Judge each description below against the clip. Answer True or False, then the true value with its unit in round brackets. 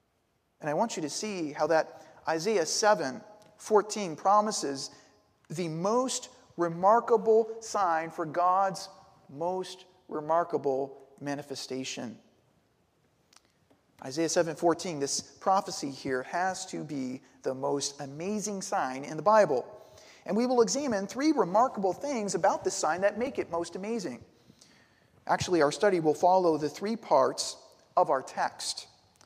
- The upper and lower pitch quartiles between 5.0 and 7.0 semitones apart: True (5.3 semitones)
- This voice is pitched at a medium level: True (180 Hz)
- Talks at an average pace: False (125 wpm)